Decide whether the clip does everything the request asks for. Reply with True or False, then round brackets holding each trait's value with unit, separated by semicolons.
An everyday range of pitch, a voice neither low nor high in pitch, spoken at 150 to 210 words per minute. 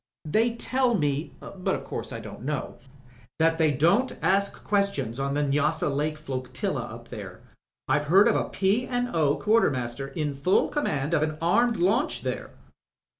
False (6.2 semitones; 155 Hz; 170 wpm)